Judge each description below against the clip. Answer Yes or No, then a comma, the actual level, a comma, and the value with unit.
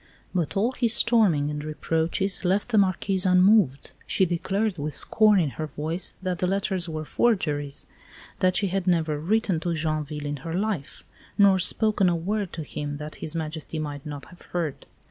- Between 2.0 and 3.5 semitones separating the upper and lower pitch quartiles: No, average, 4.4 semitones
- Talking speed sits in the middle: Yes, average, 180 wpm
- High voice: No, medium, 175 Hz